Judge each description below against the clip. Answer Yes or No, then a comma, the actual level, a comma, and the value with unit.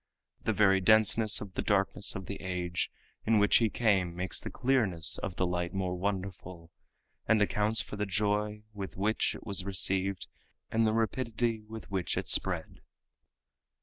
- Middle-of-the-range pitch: No, low, 100 Hz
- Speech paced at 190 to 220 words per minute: No, average, 165 wpm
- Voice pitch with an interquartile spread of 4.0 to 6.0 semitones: No, average, 2.7 semitones